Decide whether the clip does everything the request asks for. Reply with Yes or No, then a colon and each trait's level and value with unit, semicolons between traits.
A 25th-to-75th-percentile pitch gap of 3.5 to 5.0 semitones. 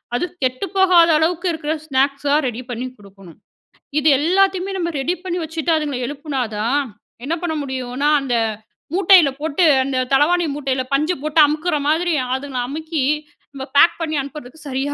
Yes: average, 4.0 semitones